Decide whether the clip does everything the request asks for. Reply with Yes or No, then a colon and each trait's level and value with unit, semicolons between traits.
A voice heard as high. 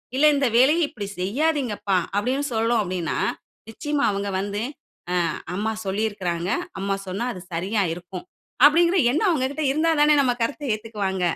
Yes: high, 220 Hz